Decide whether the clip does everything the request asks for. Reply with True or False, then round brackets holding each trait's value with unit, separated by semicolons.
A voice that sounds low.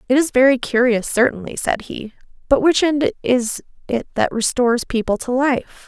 False (250 Hz)